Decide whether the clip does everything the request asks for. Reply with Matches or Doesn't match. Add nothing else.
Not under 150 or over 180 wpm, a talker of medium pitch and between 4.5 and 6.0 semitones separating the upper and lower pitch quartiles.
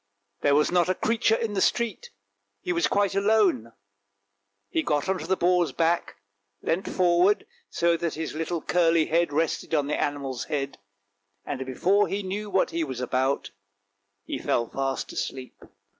Matches